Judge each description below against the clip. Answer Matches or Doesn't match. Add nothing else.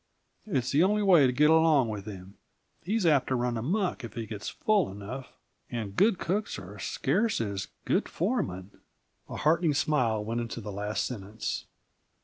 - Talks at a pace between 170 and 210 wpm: Matches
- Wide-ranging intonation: Matches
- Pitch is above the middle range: Doesn't match